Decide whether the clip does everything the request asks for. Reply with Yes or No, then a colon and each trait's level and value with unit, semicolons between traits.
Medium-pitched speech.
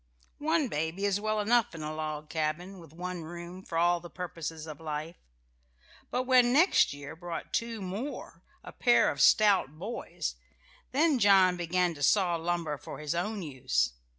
Yes: medium, 175 Hz